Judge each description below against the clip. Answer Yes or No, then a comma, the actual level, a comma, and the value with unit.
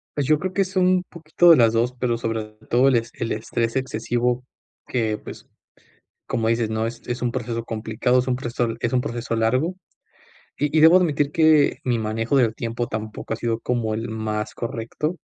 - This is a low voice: Yes, low, 120 Hz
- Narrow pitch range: No, average, 3.4 semitones